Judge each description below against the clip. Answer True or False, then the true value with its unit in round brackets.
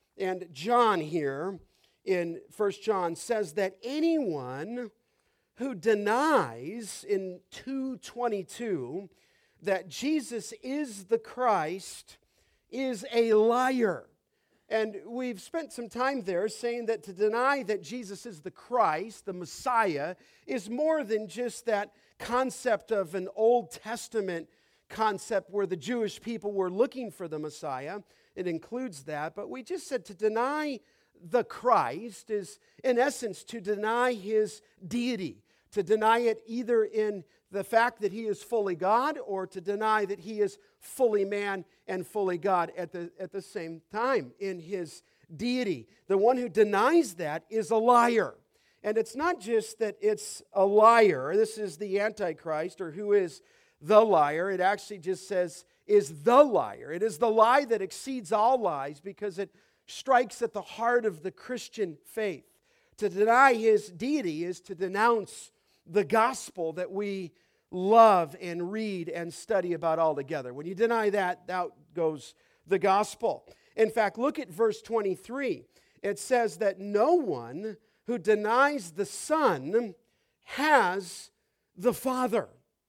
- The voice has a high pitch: True (215 Hz)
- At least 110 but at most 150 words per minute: True (145 wpm)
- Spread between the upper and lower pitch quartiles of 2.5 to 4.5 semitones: True (3.8 semitones)